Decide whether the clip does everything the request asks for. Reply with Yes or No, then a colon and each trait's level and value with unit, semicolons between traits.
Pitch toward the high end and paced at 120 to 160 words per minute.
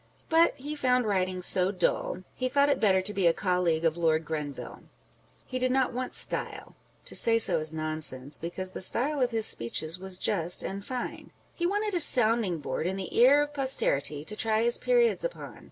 No: high, 200 Hz; average, 200 wpm